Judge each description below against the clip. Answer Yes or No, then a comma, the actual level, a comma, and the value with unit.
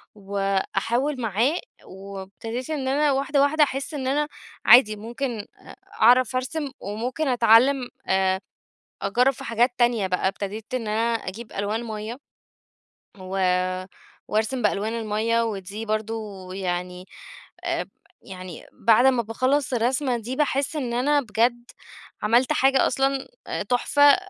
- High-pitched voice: Yes, high, 235 Hz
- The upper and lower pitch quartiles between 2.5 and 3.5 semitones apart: No, average, 4.1 semitones